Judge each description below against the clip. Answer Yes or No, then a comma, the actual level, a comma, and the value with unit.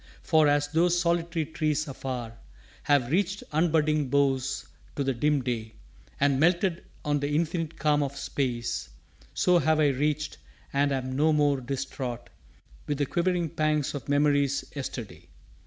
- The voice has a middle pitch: Yes, medium, 145 Hz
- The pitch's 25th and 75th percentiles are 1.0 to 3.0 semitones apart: Yes, average, 2.7 semitones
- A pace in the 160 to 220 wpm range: No, average, 145 wpm